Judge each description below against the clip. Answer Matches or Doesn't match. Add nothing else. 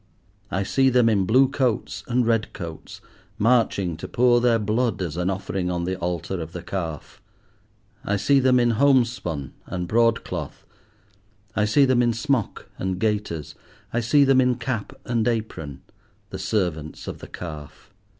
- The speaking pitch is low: Matches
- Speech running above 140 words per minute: Matches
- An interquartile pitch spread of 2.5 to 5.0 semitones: Doesn't match